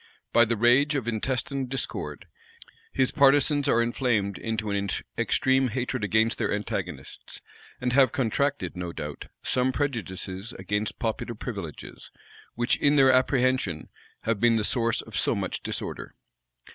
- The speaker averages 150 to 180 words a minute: No, average, 140 wpm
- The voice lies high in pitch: No, low, 120 Hz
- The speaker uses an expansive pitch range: No, average, 3.8 semitones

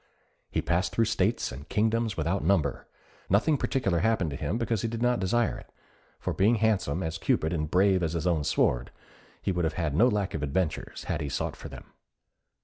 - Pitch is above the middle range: No, very low, 95 Hz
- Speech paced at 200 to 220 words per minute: Yes, fast, 205 wpm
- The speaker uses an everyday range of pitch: No, wide, 5.7 semitones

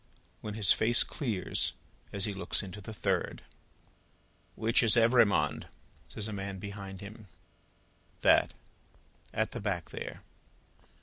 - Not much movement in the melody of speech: Yes, narrow, 2.1 semitones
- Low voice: Yes, low, 105 Hz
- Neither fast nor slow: No, slow, 125 wpm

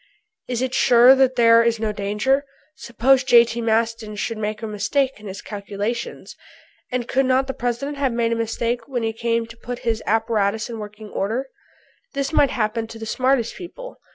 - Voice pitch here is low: No, high, 230 Hz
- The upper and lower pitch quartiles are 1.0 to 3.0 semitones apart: Yes, average, 2.7 semitones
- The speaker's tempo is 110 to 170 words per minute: No, average, 185 wpm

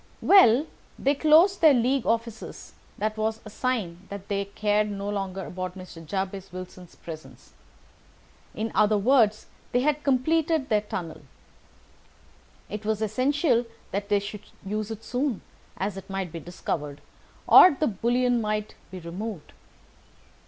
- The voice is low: No, high, 215 Hz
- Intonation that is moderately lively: Yes, average, 4.4 semitones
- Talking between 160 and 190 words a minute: No, average, 145 wpm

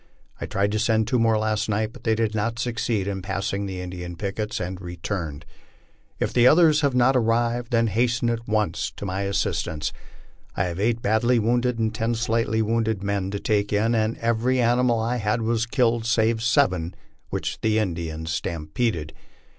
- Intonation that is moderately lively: Yes, average, 3.0 semitones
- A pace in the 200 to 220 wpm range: No, average, 185 wpm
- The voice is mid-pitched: No, low, 110 Hz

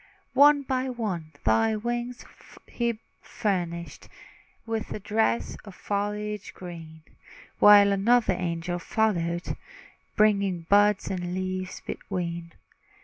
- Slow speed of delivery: Yes, slow, 100 wpm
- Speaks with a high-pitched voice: Yes, high, 200 Hz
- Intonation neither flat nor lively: Yes, average, 3.9 semitones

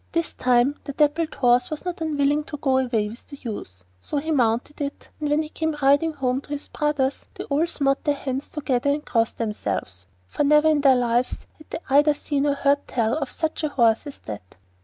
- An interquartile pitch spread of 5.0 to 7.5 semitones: No, average, 3.4 semitones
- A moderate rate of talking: No, fast, 220 wpm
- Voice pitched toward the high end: Yes, very high, 280 Hz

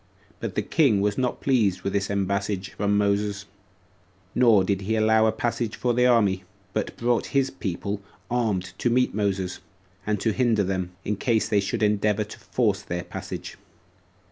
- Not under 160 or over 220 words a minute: Yes, average, 170 wpm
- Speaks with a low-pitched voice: Yes, low, 105 Hz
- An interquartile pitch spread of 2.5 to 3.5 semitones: Yes, average, 2.8 semitones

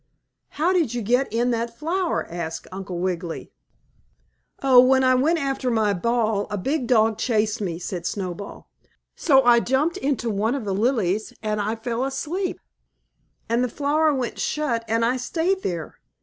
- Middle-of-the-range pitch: No, high, 235 Hz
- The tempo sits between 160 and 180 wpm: Yes, average, 165 wpm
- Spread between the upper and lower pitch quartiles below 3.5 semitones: No, average, 4.5 semitones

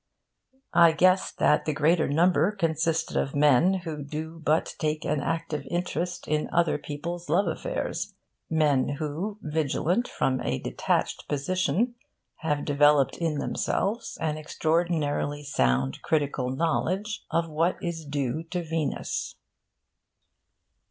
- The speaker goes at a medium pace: No, slow, 125 wpm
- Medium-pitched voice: Yes, medium, 160 Hz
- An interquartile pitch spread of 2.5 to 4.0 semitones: Yes, average, 2.9 semitones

